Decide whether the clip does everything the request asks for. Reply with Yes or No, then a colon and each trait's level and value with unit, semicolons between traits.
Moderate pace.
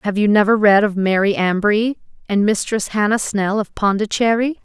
Yes: average, 170 wpm